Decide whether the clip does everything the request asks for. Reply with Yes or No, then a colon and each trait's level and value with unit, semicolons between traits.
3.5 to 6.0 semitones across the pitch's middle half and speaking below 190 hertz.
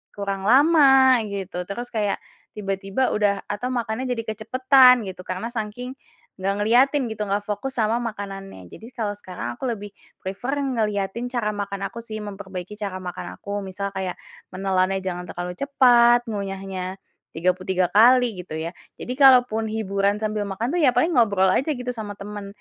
No: average, 3.8 semitones; high, 205 Hz